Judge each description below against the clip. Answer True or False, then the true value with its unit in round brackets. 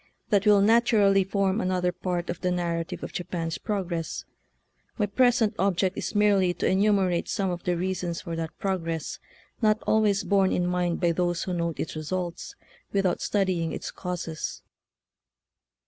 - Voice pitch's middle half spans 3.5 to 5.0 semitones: False (2.5 semitones)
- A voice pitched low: False (185 Hz)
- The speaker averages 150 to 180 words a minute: True (160 wpm)